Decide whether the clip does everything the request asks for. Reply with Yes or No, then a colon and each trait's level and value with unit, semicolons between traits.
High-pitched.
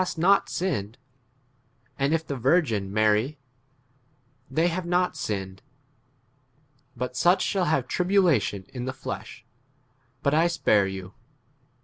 No: medium, 140 Hz